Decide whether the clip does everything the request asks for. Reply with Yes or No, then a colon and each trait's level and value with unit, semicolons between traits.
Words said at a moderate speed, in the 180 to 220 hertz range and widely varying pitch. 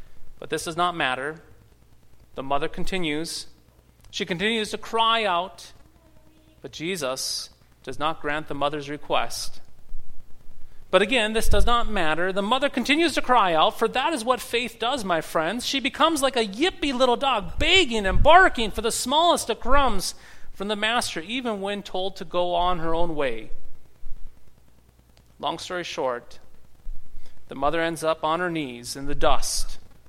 Yes: average, 160 wpm; medium, 185 Hz; wide, 8.4 semitones